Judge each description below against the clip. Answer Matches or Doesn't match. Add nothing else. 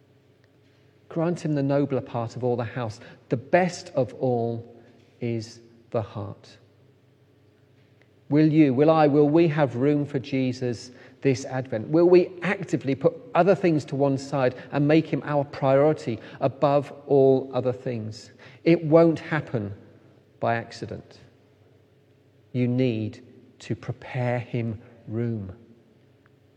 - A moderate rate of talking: Doesn't match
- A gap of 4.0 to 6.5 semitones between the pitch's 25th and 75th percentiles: Doesn't match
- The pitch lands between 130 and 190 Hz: Matches